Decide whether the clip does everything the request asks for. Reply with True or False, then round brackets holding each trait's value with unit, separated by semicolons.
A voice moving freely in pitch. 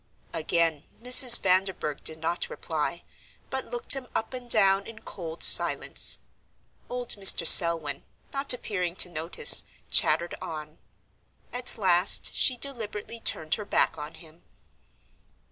True (6.4 semitones)